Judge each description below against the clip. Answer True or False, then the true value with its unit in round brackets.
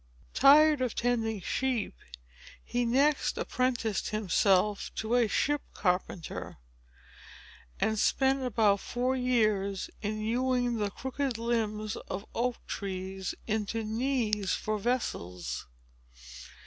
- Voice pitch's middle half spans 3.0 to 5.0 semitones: True (3.4 semitones)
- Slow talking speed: True (105 wpm)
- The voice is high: True (225 Hz)